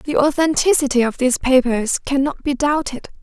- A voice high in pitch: Yes, very high, 275 Hz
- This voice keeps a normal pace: Yes, average, 150 wpm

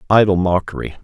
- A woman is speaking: No, male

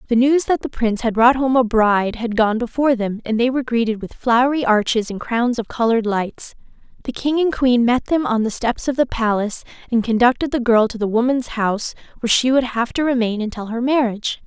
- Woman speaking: Yes, female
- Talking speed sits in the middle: No, fast, 230 wpm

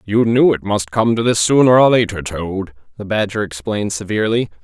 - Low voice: Yes, low, 105 Hz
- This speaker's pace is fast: No, average, 195 wpm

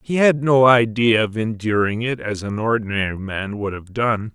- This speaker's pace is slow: No, average, 195 wpm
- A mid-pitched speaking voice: No, low, 110 Hz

